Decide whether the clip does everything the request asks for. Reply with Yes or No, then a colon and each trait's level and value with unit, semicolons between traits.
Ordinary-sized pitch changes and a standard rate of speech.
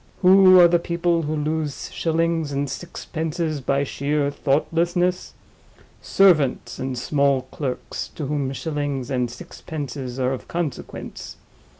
No: average, 3.5 semitones; slow, 120 wpm